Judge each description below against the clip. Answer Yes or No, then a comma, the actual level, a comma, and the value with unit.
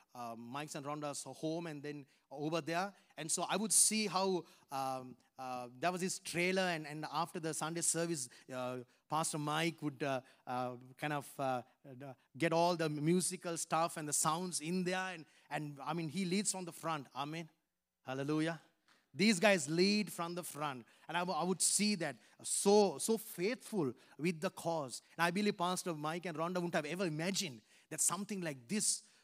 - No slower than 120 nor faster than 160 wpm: No, average, 185 wpm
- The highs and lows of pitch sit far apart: No, average, 3.8 semitones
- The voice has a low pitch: No, medium, 165 Hz